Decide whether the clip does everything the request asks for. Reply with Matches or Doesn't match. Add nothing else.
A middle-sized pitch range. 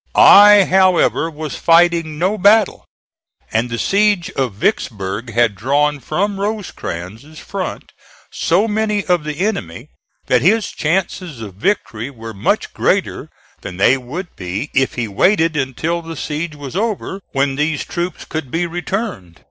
Doesn't match